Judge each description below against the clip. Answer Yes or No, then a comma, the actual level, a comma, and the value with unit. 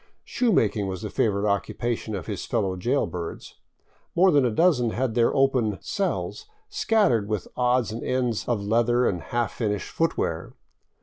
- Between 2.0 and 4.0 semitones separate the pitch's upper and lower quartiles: No, average, 4.4 semitones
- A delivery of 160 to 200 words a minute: Yes, average, 170 wpm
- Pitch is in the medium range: No, low, 120 Hz